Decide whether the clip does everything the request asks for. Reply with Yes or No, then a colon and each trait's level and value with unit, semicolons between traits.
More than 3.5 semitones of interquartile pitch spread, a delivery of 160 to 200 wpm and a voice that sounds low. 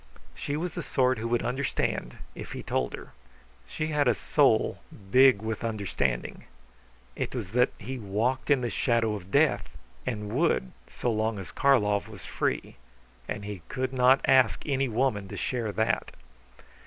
Yes: average, 4.1 semitones; average, 165 wpm; low, 115 Hz